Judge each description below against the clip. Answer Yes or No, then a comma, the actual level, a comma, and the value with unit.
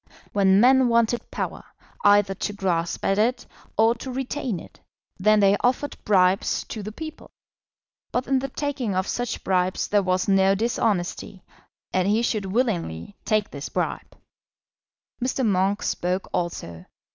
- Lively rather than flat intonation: No, average, 4.2 semitones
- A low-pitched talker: No, high, 205 Hz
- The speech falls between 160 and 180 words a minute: No, average, 145 wpm